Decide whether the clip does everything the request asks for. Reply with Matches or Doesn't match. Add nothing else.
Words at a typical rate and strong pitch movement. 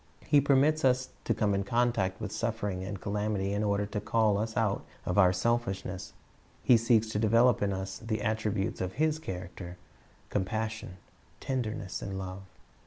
Doesn't match